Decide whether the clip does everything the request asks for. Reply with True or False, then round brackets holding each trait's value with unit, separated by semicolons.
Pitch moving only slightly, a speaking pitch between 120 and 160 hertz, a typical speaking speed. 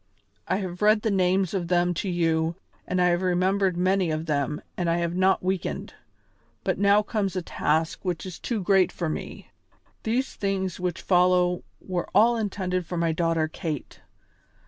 False (2.1 semitones; 180 Hz; 175 wpm)